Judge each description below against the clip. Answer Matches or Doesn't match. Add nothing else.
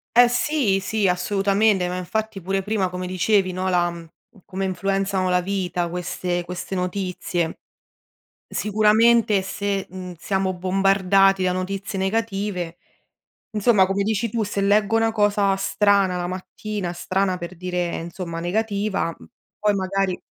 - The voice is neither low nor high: Doesn't match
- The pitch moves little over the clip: Matches